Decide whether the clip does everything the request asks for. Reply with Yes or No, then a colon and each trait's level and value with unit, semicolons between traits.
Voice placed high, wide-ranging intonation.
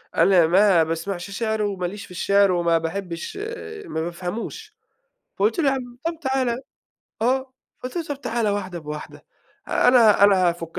Yes: high, 200 Hz; wide, 5.8 semitones